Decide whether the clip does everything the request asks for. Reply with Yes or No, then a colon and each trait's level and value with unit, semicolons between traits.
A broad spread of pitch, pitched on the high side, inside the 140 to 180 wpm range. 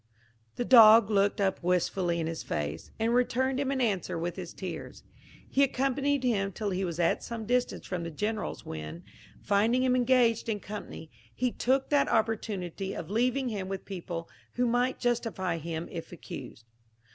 Yes: wide, 5.8 semitones; high, 210 Hz; average, 170 wpm